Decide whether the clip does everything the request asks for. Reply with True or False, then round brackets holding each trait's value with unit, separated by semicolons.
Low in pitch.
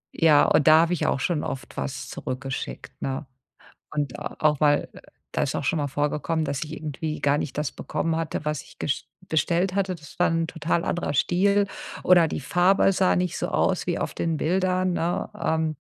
False (160 Hz)